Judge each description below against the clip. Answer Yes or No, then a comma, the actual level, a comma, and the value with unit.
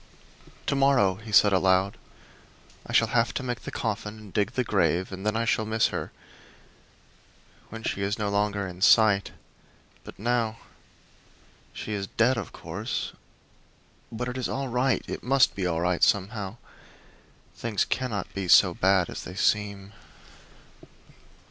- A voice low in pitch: Yes, low, 105 Hz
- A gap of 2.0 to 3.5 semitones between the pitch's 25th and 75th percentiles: Yes, average, 3.0 semitones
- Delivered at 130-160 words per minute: Yes, average, 155 wpm